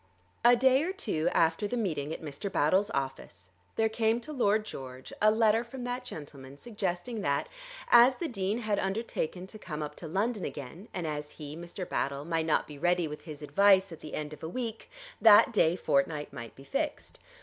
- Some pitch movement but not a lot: No, wide, 6.8 semitones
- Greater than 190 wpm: Yes, average, 200 wpm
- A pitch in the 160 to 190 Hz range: Yes, medium, 185 Hz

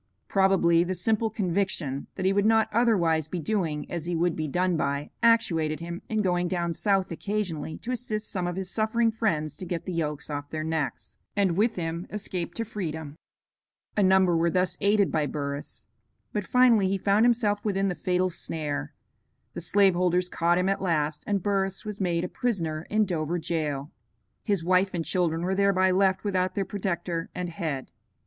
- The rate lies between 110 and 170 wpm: No, average, 185 wpm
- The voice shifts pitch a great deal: No, average, 3.4 semitones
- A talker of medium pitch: Yes, medium, 180 Hz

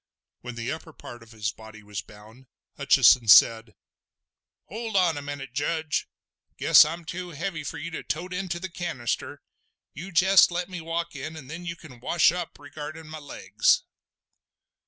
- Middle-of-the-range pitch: Yes, medium, 155 Hz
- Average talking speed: Yes, average, 170 wpm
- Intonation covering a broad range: Yes, wide, 5.9 semitones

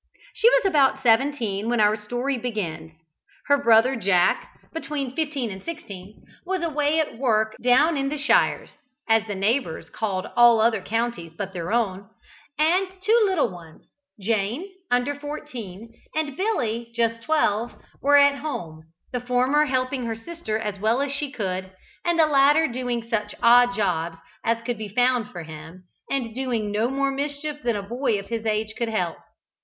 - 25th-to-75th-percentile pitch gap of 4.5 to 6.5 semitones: Yes, average, 5.1 semitones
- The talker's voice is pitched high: Yes, high, 235 Hz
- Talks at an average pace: Yes, average, 170 wpm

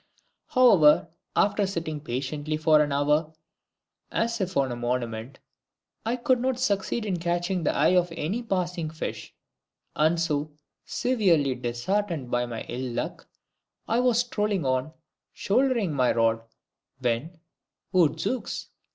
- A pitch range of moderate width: No, wide, 6.8 semitones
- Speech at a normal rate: No, slow, 130 wpm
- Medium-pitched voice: Yes, medium, 160 Hz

